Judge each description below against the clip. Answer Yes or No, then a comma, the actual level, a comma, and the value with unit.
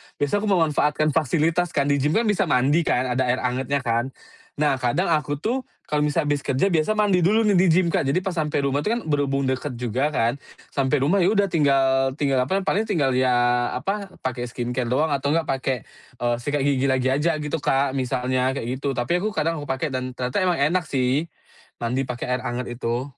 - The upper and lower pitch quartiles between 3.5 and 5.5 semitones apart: Yes, average, 4.2 semitones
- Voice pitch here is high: No, medium, 140 Hz